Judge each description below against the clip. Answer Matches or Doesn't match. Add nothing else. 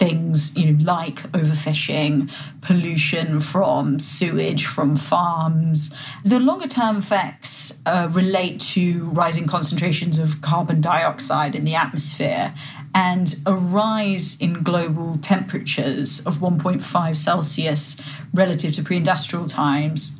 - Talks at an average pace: Doesn't match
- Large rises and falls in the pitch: Doesn't match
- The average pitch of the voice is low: Doesn't match